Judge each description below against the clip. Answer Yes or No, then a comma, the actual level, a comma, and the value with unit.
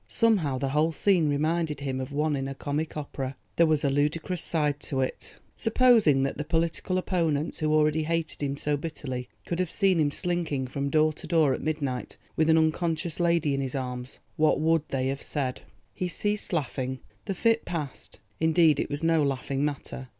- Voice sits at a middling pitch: Yes, medium, 155 Hz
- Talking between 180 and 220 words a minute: Yes, average, 185 wpm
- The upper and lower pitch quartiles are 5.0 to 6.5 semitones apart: No, average, 3.1 semitones